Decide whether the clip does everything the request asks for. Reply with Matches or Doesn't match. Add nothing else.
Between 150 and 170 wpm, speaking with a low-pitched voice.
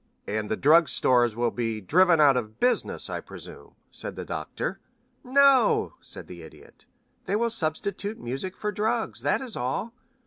Doesn't match